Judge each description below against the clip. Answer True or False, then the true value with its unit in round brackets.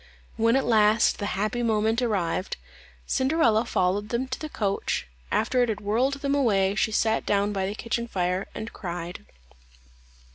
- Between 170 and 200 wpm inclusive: False (160 wpm)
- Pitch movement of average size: True (3.2 semitones)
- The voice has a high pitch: True (220 Hz)